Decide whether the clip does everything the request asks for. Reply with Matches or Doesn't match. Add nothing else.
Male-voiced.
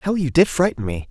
Matches